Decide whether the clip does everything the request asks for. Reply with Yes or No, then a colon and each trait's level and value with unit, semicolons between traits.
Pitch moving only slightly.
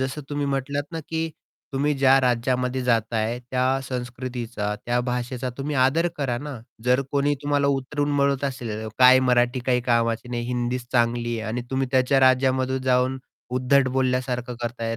Yes: narrow, 1.9 semitones